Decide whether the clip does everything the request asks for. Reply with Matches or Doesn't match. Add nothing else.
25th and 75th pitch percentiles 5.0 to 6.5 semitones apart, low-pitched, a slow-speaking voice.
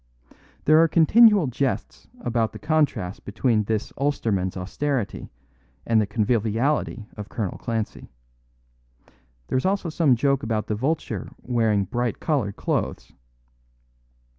Matches